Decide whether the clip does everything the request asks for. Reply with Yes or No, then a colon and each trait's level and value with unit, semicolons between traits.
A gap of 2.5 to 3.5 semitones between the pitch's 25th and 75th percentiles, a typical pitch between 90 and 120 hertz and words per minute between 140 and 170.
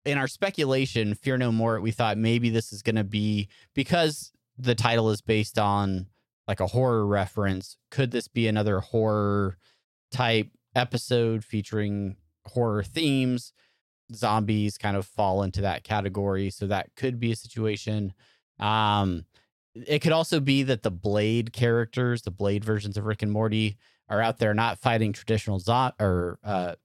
Yes: average, 2.8 semitones; low, 110 Hz; average, 160 wpm